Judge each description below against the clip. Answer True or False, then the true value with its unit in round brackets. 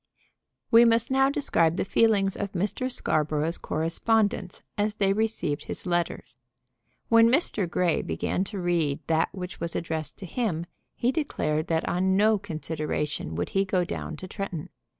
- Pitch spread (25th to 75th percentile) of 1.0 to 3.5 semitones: False (5.1 semitones)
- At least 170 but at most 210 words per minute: False (155 wpm)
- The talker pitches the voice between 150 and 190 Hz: True (185 Hz)